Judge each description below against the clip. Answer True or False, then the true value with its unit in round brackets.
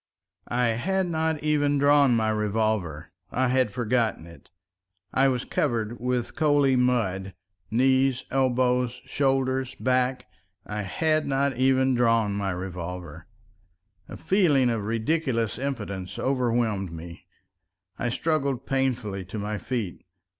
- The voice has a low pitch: True (125 Hz)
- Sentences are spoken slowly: True (115 wpm)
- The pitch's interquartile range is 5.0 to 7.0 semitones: False (4.4 semitones)